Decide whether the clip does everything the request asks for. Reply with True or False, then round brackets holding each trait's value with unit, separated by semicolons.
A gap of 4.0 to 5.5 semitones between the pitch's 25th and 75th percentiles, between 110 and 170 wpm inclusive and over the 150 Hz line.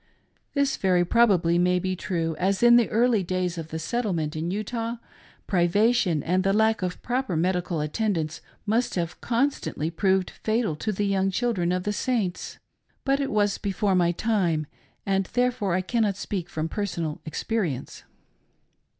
True (4.3 semitones; 160 wpm; 190 Hz)